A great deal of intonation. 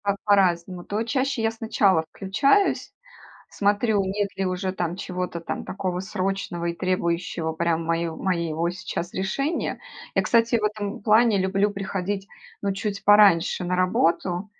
No: average, 2.8 semitones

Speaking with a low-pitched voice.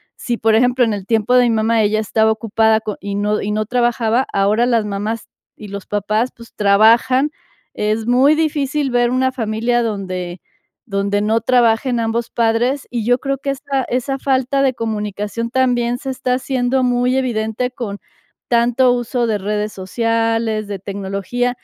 No: high, 230 Hz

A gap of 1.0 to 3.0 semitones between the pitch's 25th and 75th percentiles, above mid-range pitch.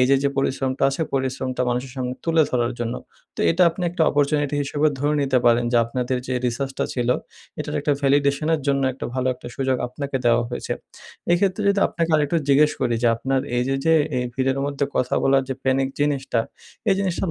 No: narrow, 2.4 semitones; low, 135 Hz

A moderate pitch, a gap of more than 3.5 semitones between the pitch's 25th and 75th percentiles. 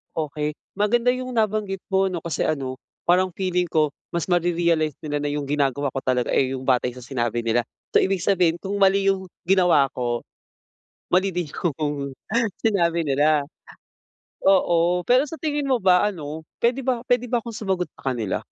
Yes: medium, 175 Hz; average, 5.3 semitones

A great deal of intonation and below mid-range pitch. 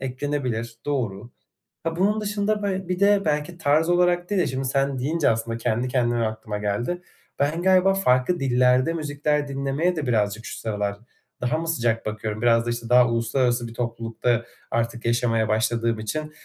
Yes: wide, 5.7 semitones; low, 125 Hz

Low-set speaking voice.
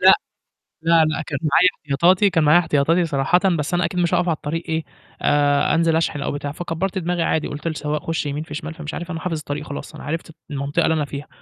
No: medium, 160 Hz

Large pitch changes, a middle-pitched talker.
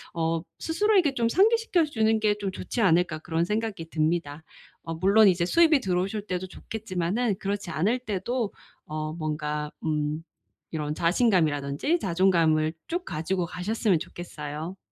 Yes: wide, 5.7 semitones; medium, 180 Hz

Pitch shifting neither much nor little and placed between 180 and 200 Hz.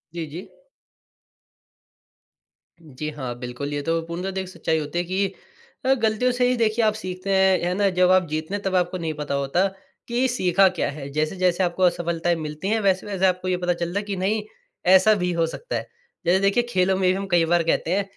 Yes: average, 3.0 semitones; medium, 185 Hz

